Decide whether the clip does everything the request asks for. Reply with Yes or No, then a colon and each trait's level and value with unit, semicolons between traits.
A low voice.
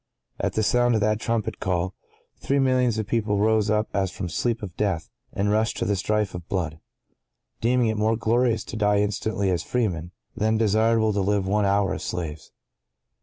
Yes: low, 105 Hz